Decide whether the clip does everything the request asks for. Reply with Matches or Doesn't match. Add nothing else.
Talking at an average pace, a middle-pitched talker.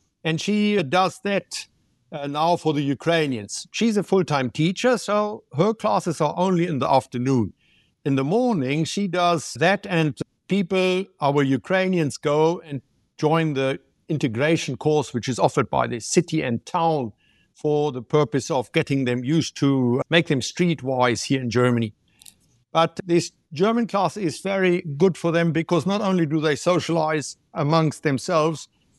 Matches